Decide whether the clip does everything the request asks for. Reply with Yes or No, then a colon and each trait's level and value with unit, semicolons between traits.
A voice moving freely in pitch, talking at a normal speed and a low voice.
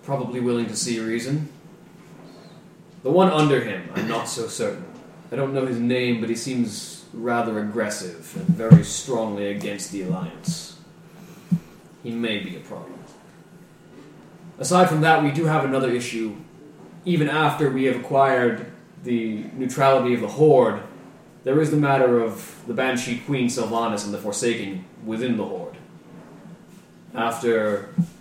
Yes: wide, 5.7 semitones; average, 145 wpm; low, 130 Hz